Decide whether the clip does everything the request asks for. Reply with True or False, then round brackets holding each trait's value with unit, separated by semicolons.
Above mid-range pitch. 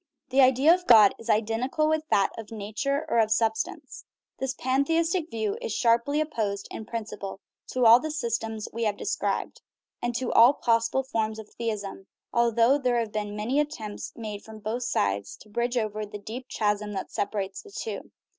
True (230 Hz)